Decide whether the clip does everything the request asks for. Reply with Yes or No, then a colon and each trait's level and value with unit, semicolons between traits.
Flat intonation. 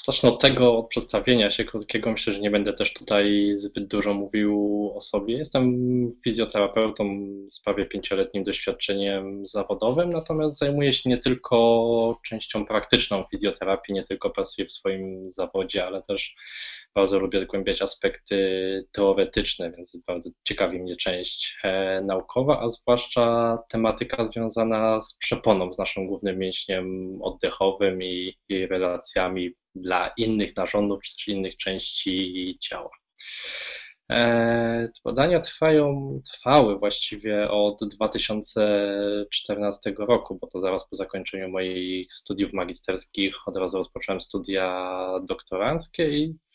No: average, 3.4 semitones